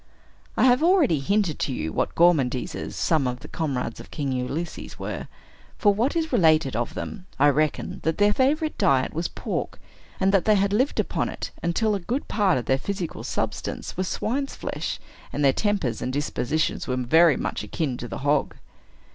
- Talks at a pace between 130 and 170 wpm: No, average, 190 wpm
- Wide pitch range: Yes, wide, 7.3 semitones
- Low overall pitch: No, medium, 165 Hz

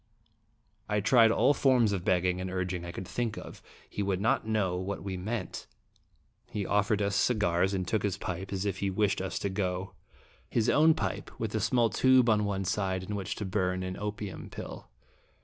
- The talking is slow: No, average, 200 wpm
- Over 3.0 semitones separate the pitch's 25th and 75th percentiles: No, narrow, 2.6 semitones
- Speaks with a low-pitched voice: Yes, low, 100 Hz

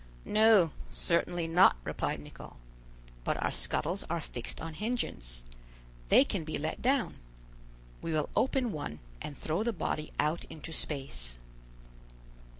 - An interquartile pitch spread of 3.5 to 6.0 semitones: Yes, wide, 5.6 semitones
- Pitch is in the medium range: Yes, medium, 165 Hz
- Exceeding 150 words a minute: No, slow, 135 wpm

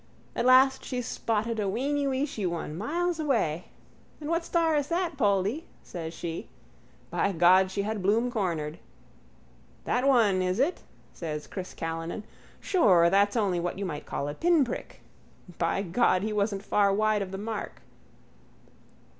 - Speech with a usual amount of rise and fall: No, wide, 6.4 semitones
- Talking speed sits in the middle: Yes, average, 155 wpm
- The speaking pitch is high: Yes, high, 205 Hz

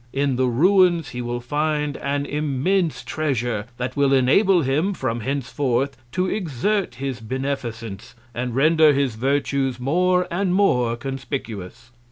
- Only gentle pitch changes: No, average, 4.2 semitones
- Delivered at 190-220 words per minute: No, slow, 135 wpm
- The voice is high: No, low, 135 Hz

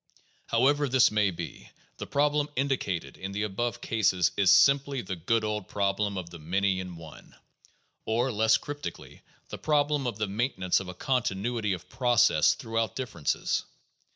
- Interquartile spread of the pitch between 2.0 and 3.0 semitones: No, wide, 5.4 semitones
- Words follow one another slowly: No, average, 160 wpm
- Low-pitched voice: Yes, low, 105 Hz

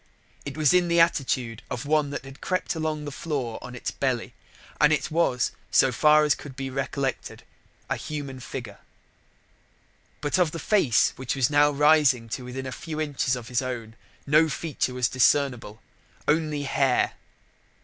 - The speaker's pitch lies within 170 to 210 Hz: No, medium, 140 Hz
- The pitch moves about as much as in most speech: Yes, average, 3.2 semitones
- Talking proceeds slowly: No, average, 170 wpm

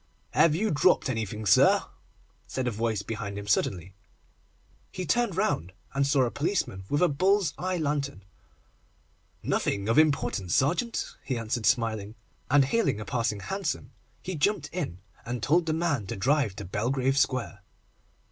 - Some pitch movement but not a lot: No, wide, 7.2 semitones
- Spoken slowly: No, average, 155 wpm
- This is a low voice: Yes, low, 130 Hz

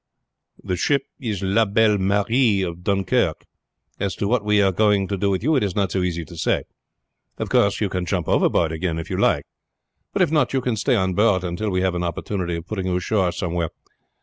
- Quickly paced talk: Yes, fast, 225 wpm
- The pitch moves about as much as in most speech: Yes, average, 3.0 semitones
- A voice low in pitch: Yes, very low, 95 Hz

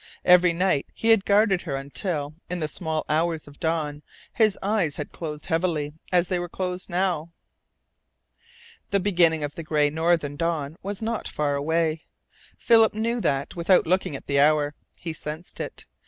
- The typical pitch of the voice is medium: Yes, medium, 165 Hz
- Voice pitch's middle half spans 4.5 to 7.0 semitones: No, average, 3.5 semitones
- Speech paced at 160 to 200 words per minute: Yes, average, 170 wpm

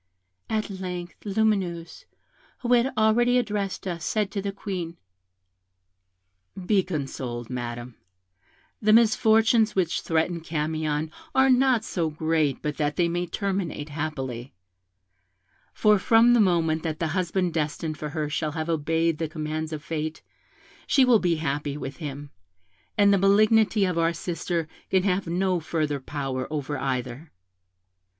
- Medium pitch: Yes, medium, 170 Hz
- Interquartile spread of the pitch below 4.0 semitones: No, average, 4.7 semitones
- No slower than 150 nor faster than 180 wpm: No, average, 140 wpm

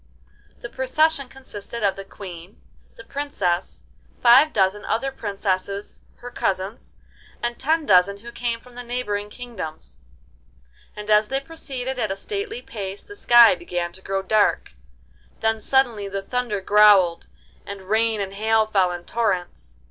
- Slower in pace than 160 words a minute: Yes, average, 150 wpm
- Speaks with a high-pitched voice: Yes, high, 210 Hz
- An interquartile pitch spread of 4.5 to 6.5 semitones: No, average, 4.1 semitones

